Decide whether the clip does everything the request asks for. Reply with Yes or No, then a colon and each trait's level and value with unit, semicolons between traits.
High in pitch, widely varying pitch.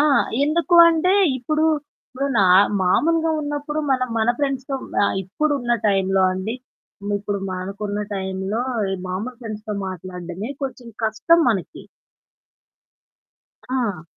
Yes: high, 225 Hz; wide, 6.7 semitones